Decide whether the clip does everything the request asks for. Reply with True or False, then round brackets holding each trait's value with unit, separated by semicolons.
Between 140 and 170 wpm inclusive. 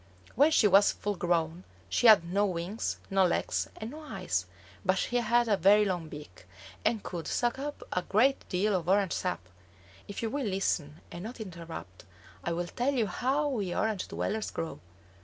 False (185 wpm)